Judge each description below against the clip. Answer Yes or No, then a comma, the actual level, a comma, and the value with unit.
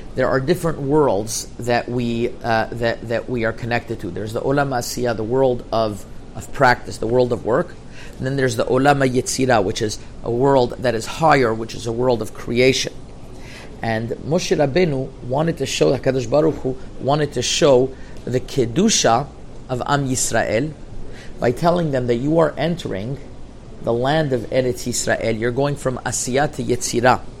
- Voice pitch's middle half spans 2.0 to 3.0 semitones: Yes, narrow, 2.6 semitones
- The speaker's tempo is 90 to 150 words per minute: No, average, 175 wpm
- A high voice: No, low, 125 Hz